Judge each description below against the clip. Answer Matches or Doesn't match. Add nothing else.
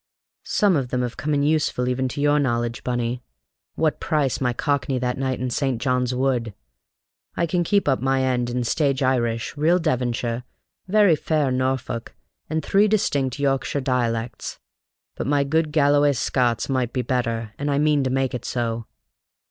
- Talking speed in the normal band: Matches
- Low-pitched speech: Matches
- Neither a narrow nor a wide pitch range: Matches